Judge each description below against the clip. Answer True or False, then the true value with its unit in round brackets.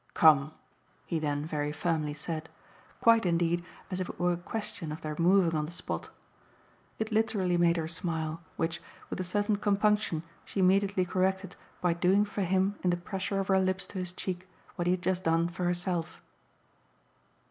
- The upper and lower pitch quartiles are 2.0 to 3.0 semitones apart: True (2.5 semitones)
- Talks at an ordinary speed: True (180 wpm)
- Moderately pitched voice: True (180 Hz)